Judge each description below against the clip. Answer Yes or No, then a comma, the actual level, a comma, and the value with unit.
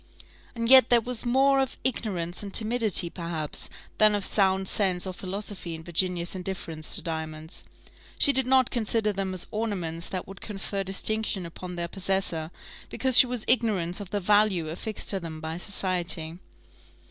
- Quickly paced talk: No, average, 165 wpm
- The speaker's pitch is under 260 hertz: Yes, high, 190 Hz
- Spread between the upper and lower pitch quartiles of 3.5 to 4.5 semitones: Yes, average, 4.1 semitones